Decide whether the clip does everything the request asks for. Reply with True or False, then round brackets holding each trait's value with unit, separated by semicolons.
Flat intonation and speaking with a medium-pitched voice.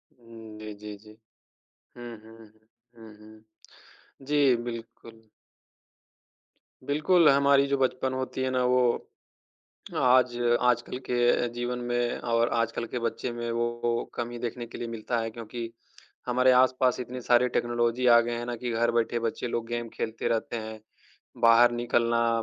False (1.4 semitones; 120 Hz)